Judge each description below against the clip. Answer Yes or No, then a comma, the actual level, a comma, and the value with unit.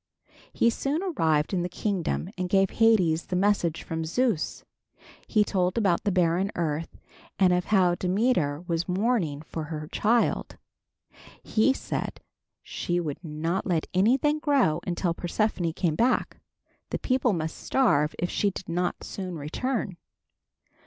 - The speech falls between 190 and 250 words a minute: No, average, 145 wpm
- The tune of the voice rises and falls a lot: No, average, 4.7 semitones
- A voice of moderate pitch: Yes, medium, 180 Hz